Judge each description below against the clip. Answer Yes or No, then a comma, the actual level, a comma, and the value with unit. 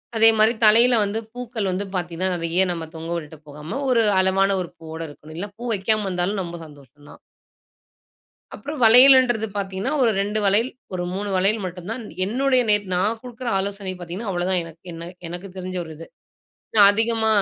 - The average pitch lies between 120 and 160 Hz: No, high, 195 Hz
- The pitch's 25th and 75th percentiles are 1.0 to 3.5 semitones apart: No, average, 4.3 semitones